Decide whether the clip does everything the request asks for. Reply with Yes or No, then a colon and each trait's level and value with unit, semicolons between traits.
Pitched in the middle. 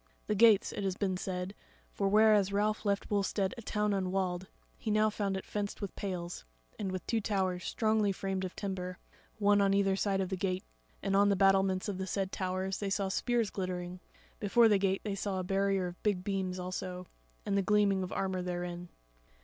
No: high, 195 Hz